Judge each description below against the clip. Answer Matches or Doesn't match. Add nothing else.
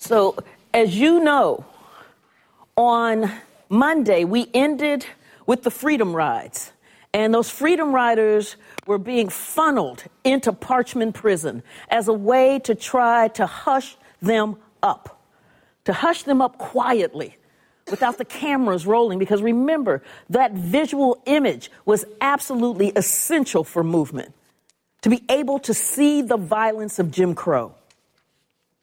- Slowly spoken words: Matches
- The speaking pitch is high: Matches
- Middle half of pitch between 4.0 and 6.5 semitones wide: Matches